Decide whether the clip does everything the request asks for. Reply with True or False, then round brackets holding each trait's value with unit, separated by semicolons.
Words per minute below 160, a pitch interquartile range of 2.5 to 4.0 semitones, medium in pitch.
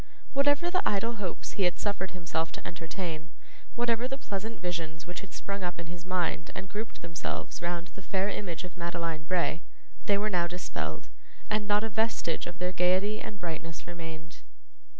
False (180 wpm; 3.3 semitones; 180 Hz)